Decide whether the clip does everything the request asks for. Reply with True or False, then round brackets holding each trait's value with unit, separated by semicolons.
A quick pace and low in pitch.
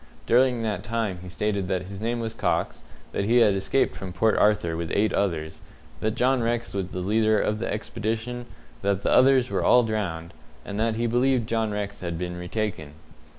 False (195 wpm; 105 Hz)